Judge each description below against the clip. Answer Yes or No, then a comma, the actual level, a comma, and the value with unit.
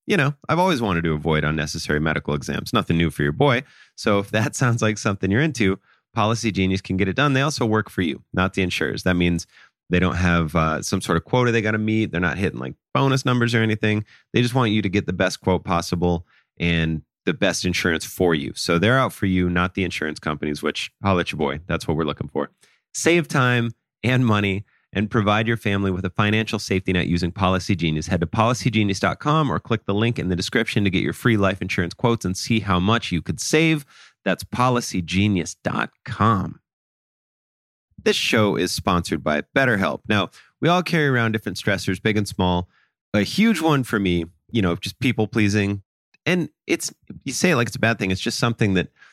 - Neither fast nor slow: No, fast, 215 wpm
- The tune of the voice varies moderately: Yes, average, 4.4 semitones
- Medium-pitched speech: No, low, 100 Hz